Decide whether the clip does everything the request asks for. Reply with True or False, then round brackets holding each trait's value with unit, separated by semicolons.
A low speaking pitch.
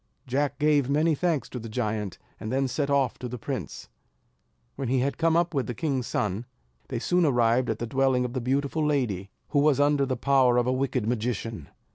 True (130 Hz)